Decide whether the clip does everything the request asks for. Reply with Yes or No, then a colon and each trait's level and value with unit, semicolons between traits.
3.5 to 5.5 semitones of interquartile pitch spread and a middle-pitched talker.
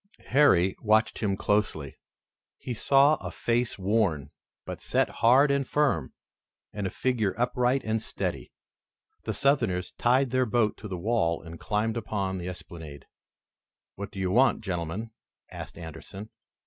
No: average, 5.2 semitones; low, 105 Hz